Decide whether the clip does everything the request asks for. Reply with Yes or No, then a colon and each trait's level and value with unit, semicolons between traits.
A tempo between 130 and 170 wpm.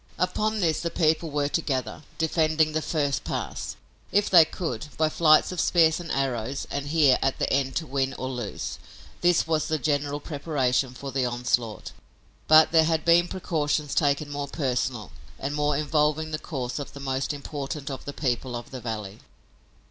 No: average, 180 wpm